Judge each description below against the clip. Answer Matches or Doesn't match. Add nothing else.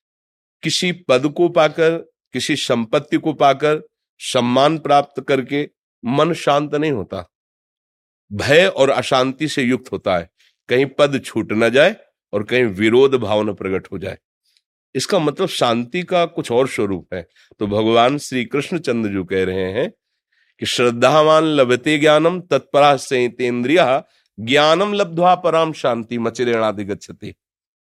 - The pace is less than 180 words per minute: Matches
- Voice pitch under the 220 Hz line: Matches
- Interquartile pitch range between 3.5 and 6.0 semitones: Matches